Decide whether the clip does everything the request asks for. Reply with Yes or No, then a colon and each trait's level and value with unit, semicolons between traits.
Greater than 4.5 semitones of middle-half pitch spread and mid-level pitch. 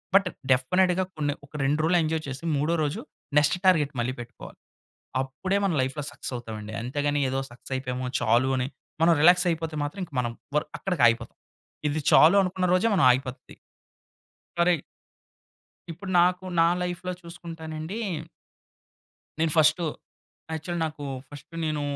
Yes: average, 4.9 semitones; medium, 155 Hz